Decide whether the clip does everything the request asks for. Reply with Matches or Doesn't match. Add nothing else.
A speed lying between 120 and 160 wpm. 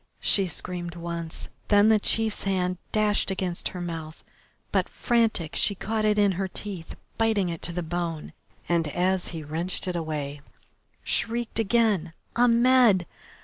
Matches